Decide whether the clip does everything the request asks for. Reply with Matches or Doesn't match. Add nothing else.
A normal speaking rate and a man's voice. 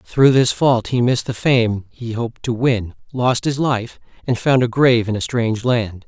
Doesn't match